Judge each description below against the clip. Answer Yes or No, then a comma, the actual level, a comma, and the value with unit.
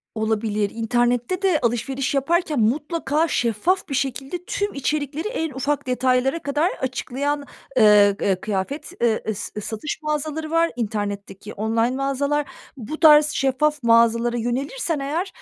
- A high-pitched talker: Yes, very high, 270 Hz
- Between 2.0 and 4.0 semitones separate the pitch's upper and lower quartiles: No, average, 4.7 semitones